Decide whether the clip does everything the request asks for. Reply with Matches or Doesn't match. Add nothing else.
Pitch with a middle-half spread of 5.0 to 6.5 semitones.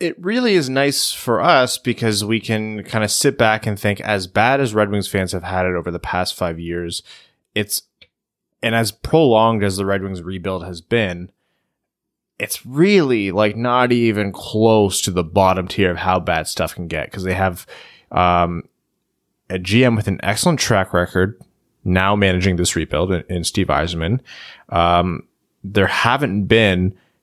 Doesn't match